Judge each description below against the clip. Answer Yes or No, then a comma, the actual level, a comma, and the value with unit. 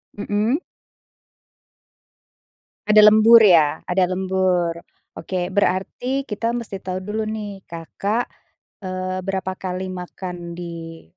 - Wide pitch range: No, average, 2.8 semitones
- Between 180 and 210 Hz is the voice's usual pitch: Yes, high, 190 Hz